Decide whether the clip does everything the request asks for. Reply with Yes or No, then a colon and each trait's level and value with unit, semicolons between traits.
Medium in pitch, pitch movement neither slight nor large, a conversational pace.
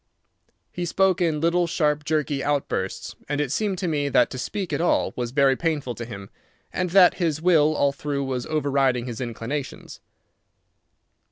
Yes: medium, 145 Hz; average, 4.2 semitones; average, 170 wpm